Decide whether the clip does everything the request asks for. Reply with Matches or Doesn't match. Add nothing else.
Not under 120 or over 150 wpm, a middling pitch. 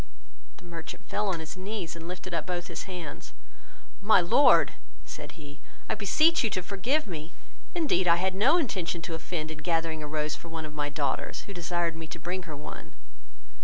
Doesn't match